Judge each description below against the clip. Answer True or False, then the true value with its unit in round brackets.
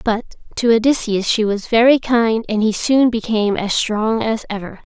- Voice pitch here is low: False (225 Hz)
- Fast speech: False (185 wpm)